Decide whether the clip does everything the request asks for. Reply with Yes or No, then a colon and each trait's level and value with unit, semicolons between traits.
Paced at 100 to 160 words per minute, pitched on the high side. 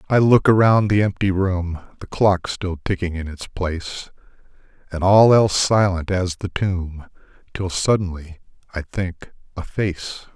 No: average, 150 wpm; very low, 90 Hz